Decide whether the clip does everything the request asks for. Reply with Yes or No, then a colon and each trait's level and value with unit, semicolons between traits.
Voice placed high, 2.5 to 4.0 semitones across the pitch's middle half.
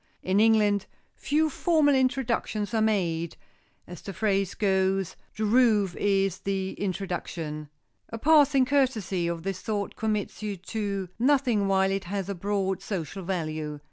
Yes: high, 200 Hz; average, 2.8 semitones